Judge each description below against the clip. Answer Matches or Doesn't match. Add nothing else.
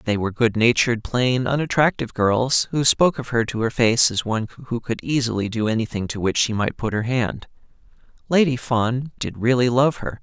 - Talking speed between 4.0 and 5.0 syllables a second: Doesn't match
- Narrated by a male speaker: Matches